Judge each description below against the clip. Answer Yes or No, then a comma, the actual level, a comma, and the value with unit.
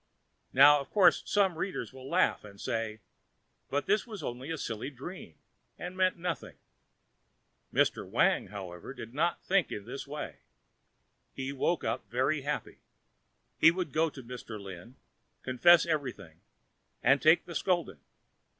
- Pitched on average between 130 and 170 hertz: Yes, medium, 140 Hz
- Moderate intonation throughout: No, wide, 6.7 semitones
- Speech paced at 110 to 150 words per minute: Yes, average, 145 wpm